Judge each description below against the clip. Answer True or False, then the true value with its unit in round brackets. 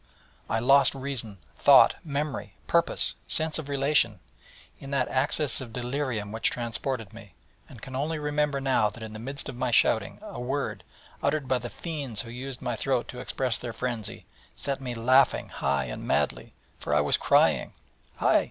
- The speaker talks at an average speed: True (175 wpm)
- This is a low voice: True (130 Hz)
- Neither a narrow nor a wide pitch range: True (3.3 semitones)